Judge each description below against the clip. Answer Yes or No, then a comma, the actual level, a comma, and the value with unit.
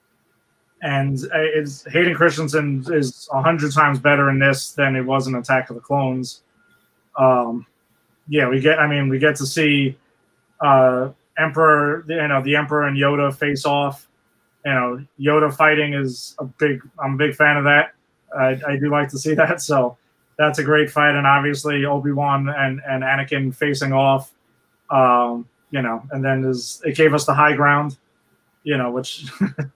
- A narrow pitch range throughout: Yes, narrow, 2.0 semitones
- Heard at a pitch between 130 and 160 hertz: Yes, medium, 140 Hz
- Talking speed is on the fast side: No, average, 170 wpm